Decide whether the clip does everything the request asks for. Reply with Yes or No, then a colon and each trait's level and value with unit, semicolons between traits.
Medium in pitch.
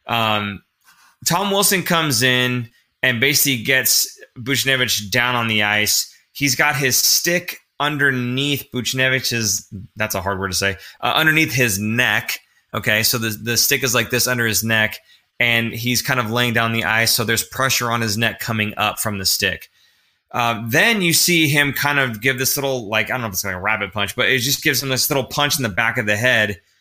No: low, 120 Hz